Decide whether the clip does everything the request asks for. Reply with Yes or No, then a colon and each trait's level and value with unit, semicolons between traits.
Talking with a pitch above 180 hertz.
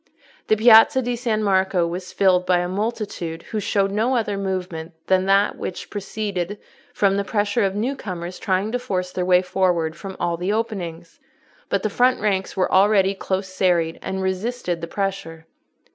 Yes: high, 190 Hz